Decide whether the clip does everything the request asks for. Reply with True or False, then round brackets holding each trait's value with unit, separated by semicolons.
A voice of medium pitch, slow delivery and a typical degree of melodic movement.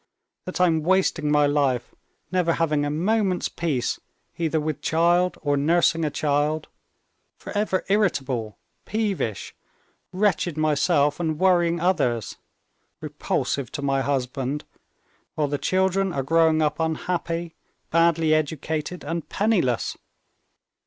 True (160 Hz; 115 wpm; 3.5 semitones)